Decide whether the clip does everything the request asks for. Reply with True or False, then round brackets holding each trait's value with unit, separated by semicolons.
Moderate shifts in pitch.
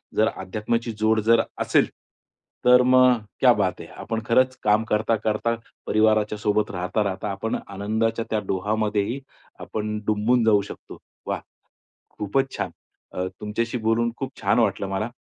False (1.9 semitones)